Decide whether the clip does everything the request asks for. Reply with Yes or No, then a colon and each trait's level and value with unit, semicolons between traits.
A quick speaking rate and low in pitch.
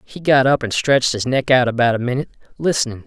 Yes: fast, 235 wpm; low, 125 Hz